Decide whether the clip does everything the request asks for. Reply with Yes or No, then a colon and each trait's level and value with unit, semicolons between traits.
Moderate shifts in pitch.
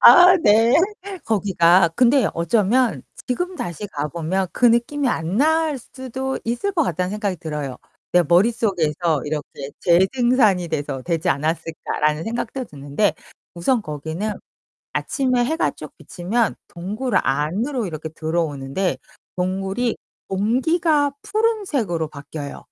No: wide, 7.6 semitones